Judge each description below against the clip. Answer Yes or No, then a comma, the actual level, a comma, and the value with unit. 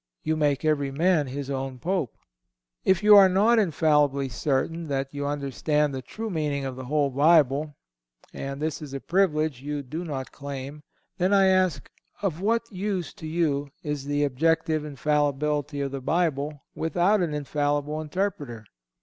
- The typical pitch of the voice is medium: Yes, medium, 150 Hz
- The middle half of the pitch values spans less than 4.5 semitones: Yes, average, 3.1 semitones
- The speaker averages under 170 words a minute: Yes, average, 155 wpm